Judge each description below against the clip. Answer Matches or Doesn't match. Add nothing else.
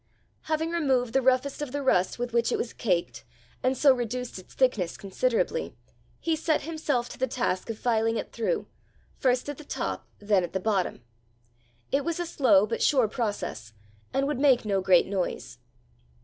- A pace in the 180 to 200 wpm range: Matches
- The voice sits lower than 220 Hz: Doesn't match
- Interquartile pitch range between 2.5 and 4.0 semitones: Doesn't match